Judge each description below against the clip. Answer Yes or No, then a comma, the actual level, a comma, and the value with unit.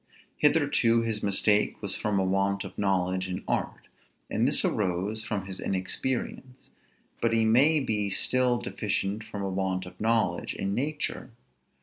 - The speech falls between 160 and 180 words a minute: No, average, 150 wpm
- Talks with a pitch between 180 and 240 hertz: No, low, 105 Hz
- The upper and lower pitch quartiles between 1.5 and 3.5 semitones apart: Yes, average, 3.1 semitones